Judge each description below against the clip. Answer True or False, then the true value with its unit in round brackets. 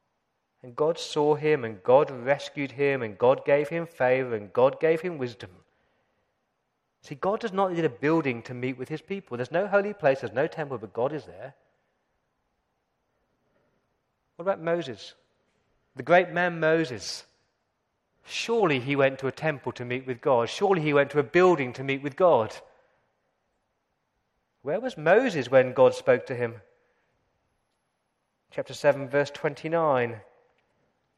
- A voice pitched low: False (145 Hz)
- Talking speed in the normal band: True (150 wpm)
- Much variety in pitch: False (4.9 semitones)